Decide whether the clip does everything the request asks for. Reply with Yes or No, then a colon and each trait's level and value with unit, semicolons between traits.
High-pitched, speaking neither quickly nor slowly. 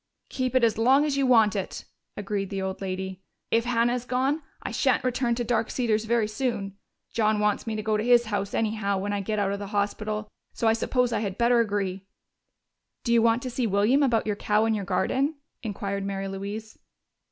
No: high, 215 Hz; fast, 215 wpm